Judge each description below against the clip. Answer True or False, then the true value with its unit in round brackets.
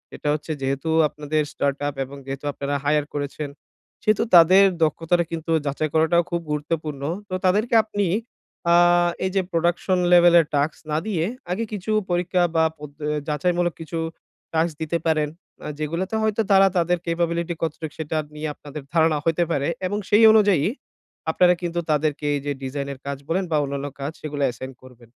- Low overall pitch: False (160 Hz)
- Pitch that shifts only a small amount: False (3.2 semitones)